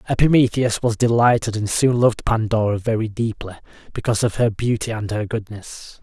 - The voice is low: Yes, low, 110 Hz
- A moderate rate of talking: Yes, average, 160 wpm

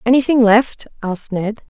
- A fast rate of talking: No, slow, 135 wpm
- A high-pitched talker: Yes, high, 225 Hz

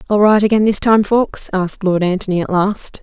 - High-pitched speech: Yes, high, 200 Hz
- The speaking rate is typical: No, fast, 220 wpm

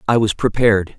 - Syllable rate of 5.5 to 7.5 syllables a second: Yes, 6.0 syllables/s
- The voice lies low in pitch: Yes, low, 110 Hz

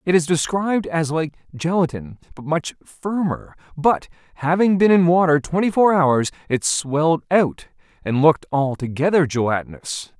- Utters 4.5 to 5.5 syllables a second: Yes, 4.9 syllables/s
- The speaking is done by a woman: No, male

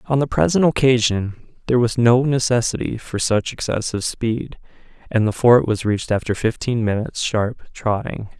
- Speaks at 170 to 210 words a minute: No, average, 155 wpm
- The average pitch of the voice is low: Yes, low, 115 Hz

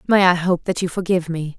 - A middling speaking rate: No, fast, 265 wpm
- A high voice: No, medium, 175 Hz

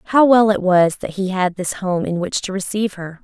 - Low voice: No, high, 190 Hz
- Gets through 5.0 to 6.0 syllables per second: Yes, 5.4 syllables/s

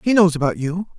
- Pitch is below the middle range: No, medium, 175 Hz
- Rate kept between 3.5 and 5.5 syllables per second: No, 6.1 syllables/s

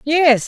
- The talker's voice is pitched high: Yes, very high, 285 Hz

